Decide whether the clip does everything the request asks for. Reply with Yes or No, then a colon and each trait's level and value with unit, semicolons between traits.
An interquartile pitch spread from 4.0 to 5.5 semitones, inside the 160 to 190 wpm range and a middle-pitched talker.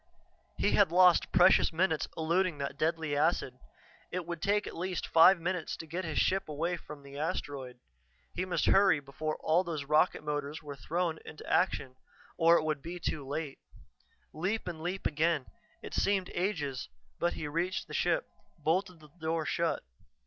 No: average, 3.2 semitones; average, 170 wpm; medium, 165 Hz